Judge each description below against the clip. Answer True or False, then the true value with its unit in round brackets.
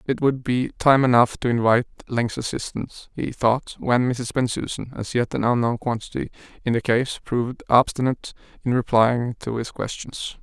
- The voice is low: True (120 Hz)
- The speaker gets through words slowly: False (155 wpm)